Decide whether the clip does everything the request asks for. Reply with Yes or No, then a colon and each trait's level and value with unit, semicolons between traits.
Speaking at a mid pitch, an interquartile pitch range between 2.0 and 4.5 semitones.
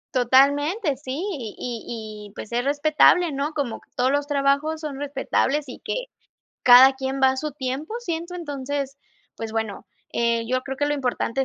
No: very high, 275 Hz; average, 2.9 semitones